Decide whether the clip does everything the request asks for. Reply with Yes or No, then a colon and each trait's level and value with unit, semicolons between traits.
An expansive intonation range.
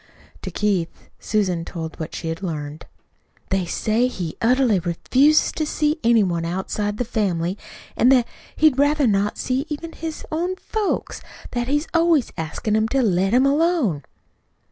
Yes: wide, 8.2 semitones